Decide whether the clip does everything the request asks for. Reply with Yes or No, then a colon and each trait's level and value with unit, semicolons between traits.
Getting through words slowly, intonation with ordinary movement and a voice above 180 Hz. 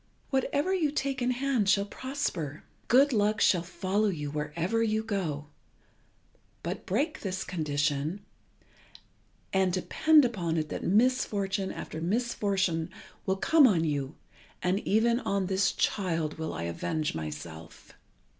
No: slow, 130 wpm; wide, 6.5 semitones; high, 190 Hz